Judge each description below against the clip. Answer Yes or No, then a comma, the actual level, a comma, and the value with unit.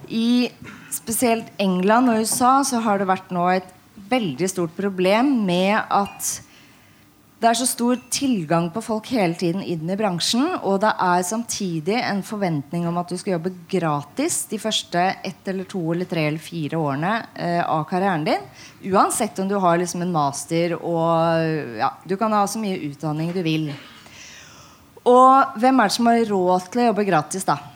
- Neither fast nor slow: Yes, average, 180 wpm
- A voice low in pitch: No, high, 190 Hz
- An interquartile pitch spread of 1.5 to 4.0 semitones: No, average, 4.7 semitones